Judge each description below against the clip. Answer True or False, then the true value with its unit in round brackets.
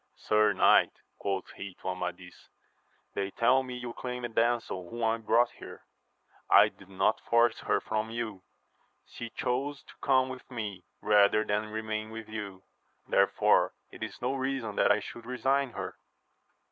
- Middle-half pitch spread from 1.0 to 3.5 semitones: True (3.2 semitones)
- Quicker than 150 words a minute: True (160 wpm)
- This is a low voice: True (110 Hz)